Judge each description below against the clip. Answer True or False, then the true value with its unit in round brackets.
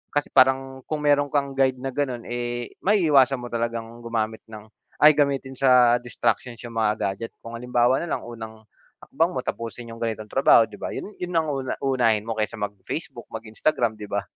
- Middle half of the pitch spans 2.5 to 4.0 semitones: True (3.1 semitones)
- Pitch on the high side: False (120 Hz)